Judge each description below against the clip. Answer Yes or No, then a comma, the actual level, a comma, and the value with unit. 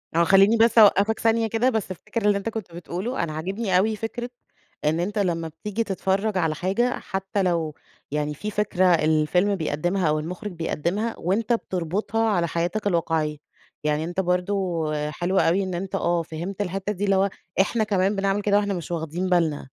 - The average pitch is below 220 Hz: Yes, high, 190 Hz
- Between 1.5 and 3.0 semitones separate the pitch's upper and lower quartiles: No, average, 3.6 semitones